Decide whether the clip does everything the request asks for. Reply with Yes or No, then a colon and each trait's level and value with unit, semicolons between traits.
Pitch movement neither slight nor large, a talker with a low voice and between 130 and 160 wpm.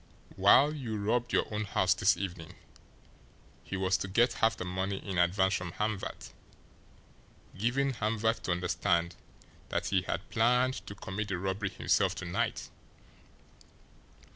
Yes: average, 3.3 semitones; low, 100 Hz; average, 140 wpm